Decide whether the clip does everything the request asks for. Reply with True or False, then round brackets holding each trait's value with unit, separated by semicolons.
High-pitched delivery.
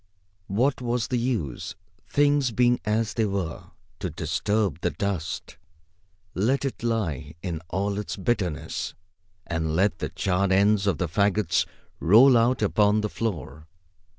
False (100 Hz)